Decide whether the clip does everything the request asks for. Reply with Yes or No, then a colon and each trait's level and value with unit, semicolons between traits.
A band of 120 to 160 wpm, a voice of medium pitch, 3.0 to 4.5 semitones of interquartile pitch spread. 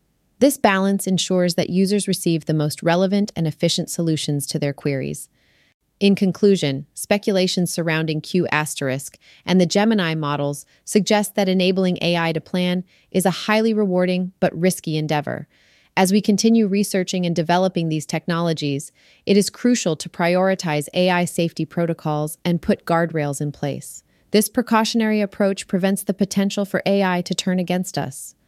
Yes: average, 150 wpm; medium, 180 Hz; average, 3.6 semitones